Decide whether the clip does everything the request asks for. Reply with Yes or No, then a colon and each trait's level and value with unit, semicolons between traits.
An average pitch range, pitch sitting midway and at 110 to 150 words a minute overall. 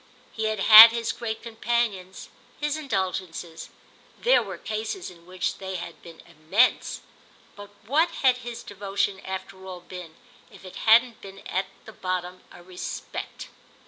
No: average, 4.0 semitones; high, 195 Hz; average, 140 wpm